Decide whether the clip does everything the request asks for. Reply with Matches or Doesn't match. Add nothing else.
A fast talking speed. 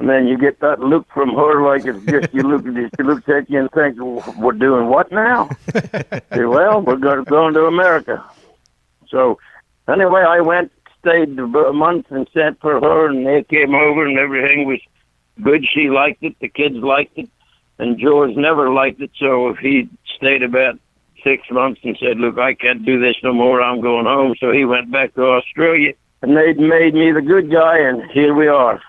Matches